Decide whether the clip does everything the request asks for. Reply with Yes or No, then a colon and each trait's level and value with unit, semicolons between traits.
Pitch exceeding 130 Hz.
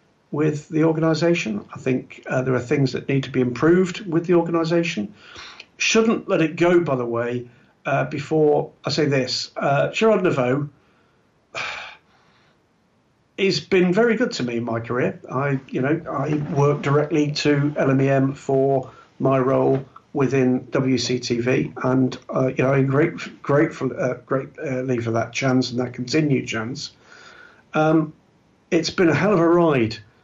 Yes: medium, 140 Hz